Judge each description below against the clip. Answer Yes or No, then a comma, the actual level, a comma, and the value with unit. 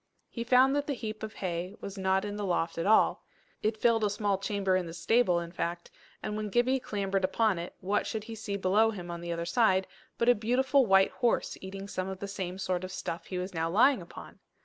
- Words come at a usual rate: No, fast, 240 wpm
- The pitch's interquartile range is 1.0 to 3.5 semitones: Yes, average, 3.2 semitones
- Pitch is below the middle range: No, high, 200 Hz